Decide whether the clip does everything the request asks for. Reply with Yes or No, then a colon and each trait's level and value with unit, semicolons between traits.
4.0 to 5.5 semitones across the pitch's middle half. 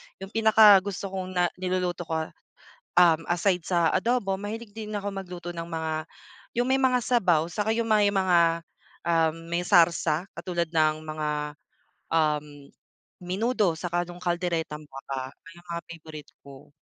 No: average, 3.4 semitones